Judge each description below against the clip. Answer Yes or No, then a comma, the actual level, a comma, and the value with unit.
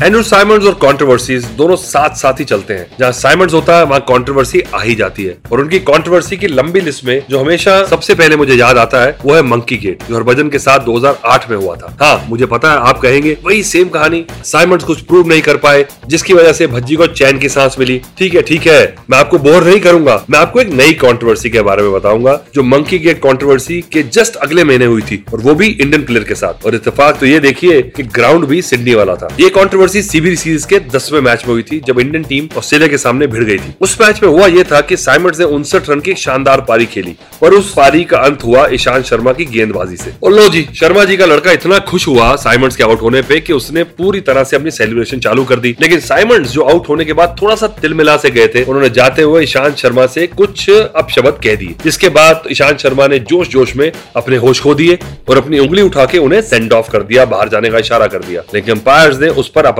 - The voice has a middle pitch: Yes, medium, 145 Hz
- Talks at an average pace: No, fast, 240 wpm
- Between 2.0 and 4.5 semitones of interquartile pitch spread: No, average, 4.9 semitones